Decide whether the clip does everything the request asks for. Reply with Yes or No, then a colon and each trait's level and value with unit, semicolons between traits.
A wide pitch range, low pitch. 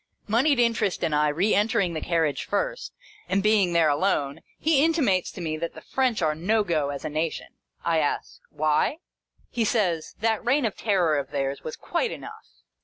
No: wide, 6.4 semitones; medium, 185 Hz